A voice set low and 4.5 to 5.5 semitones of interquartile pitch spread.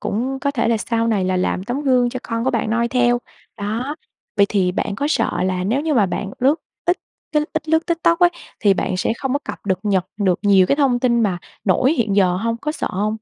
No: high, 230 Hz; average, 5.1 semitones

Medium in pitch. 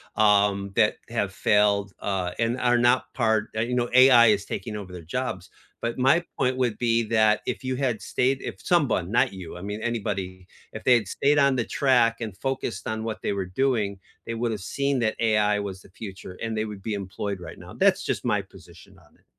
No: low, 110 Hz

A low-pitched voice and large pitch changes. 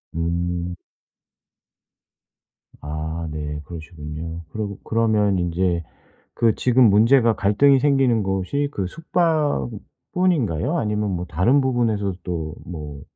Yes: low, 100 Hz; wide, 6.5 semitones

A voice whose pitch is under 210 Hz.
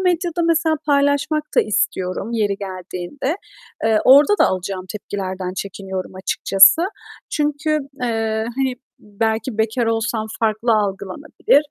No: high, 220 Hz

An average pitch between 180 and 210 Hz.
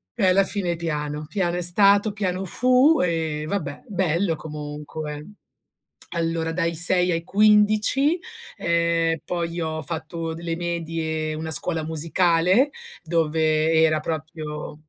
No: medium, 165 Hz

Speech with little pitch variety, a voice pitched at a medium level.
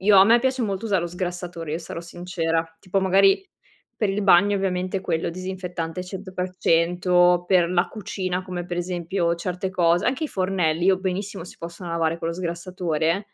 Yes: narrow, 2.0 semitones; medium, 180 Hz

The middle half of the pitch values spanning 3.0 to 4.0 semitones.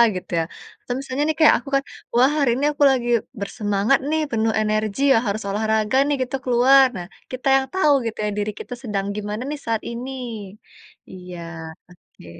No: average, 4.4 semitones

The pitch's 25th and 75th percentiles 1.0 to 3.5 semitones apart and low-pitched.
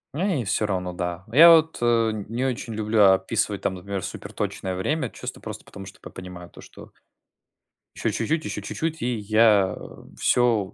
No: average, 4.5 semitones; low, 110 Hz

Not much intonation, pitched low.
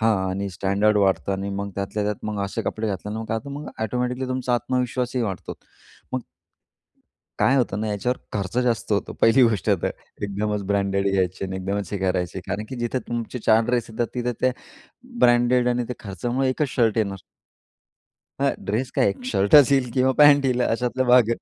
No: average, 3.8 semitones; low, 110 Hz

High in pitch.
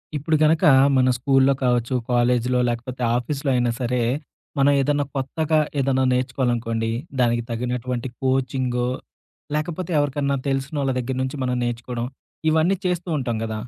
No: low, 130 Hz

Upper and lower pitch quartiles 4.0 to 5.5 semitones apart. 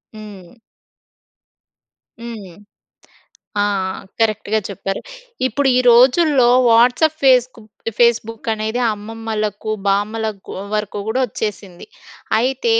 No: narrow, 2.6 semitones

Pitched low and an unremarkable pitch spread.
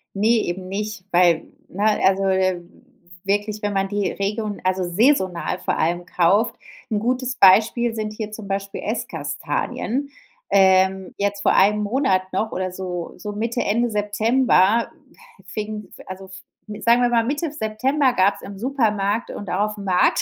No: high, 205 Hz; average, 3.1 semitones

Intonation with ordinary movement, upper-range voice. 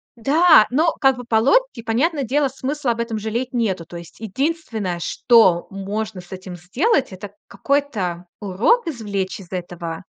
No: wide, 6.4 semitones; high, 225 Hz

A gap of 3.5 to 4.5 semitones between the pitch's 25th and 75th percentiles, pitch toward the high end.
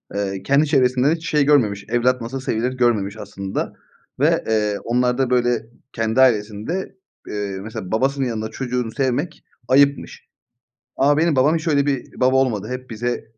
No: average, 3.8 semitones; low, 125 Hz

